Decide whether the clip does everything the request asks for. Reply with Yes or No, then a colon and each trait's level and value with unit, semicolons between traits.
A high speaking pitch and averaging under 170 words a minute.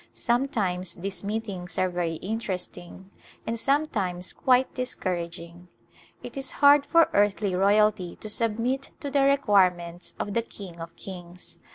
Yes: high, 200 Hz; average, 140 wpm